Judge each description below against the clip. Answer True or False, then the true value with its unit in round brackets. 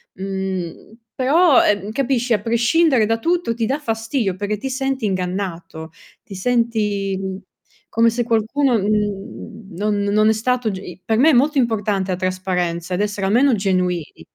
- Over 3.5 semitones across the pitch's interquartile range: True (4.0 semitones)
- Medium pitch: False (210 Hz)